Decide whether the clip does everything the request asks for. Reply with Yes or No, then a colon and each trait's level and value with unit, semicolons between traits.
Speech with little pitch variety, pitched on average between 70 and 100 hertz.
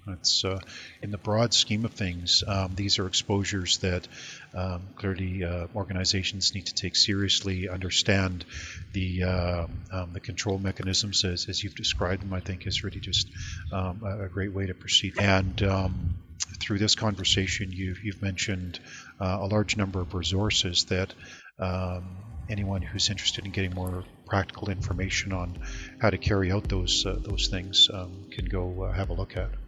Yes: narrow, 1.6 semitones; very low, 95 Hz